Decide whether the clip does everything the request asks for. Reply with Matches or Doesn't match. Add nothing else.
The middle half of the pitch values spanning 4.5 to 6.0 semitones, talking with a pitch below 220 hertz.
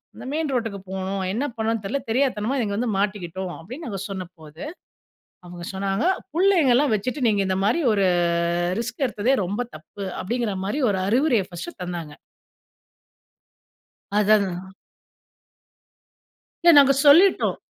Matches